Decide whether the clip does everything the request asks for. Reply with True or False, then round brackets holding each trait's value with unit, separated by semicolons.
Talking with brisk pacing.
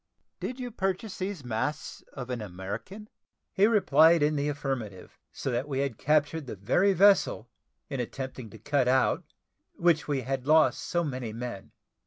False (165 wpm)